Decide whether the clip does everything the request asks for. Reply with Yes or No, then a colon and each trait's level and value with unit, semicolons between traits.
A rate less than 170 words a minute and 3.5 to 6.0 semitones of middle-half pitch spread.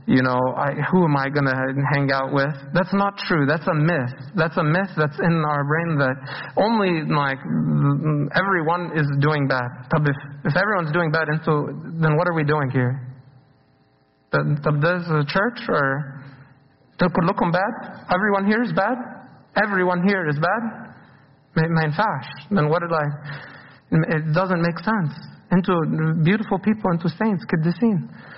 Yes: average, 160 wpm; average, 4.7 semitones